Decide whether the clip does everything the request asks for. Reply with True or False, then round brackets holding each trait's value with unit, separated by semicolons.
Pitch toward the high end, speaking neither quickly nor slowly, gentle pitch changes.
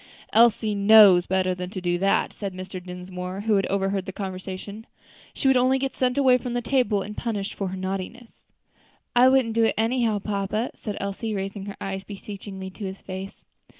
False (200 Hz; 190 wpm; 3.0 semitones)